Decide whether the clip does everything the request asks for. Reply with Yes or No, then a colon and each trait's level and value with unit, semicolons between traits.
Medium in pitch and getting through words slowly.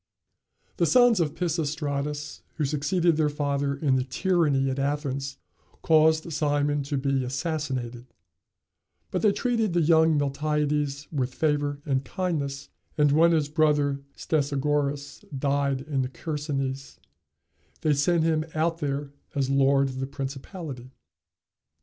Yes: medium, 145 Hz; slow, 130 wpm